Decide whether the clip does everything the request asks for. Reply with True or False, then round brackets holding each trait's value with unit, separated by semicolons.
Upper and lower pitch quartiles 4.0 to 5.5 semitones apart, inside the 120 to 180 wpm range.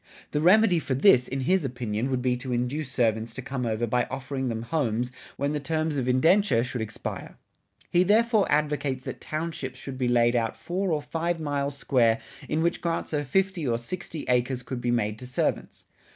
False (4.6 semitones; 195 wpm)